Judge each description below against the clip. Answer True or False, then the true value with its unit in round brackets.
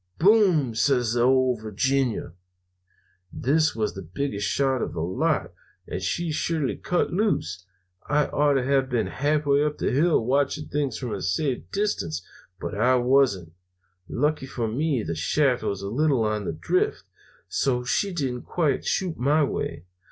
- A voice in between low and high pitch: False (130 Hz)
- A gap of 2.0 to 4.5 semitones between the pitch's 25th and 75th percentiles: False (5.3 semitones)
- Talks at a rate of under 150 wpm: False (160 wpm)